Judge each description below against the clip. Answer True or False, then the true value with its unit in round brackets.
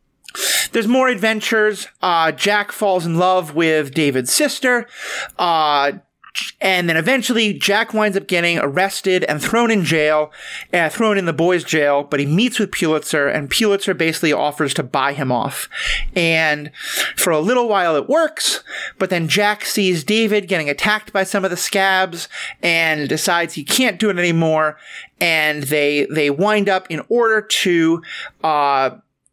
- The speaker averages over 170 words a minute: False (160 wpm)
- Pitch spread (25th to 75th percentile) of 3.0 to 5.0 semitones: False (5.5 semitones)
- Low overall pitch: False (175 Hz)